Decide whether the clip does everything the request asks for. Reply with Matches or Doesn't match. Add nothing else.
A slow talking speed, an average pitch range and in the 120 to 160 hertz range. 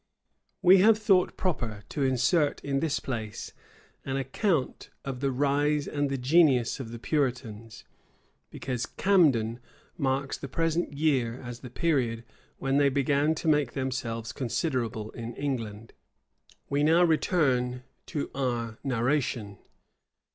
Matches